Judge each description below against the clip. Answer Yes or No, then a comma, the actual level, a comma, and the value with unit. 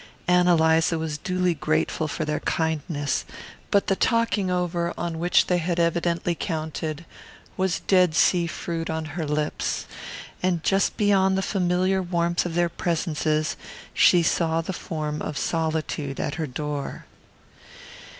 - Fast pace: No, average, 140 wpm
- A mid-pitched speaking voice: Yes, medium, 170 Hz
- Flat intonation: Yes, narrow, 2.2 semitones